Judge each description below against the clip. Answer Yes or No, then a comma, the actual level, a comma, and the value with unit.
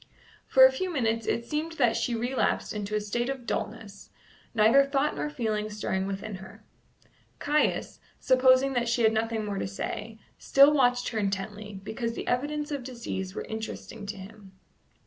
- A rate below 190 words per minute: Yes, average, 170 wpm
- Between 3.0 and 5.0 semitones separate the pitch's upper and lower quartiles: Yes, average, 4.2 semitones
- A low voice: No, high, 230 Hz